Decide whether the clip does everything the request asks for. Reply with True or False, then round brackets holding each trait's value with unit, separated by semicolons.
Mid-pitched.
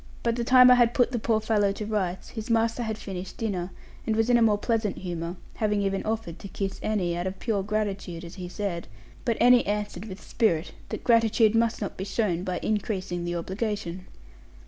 False (210 Hz)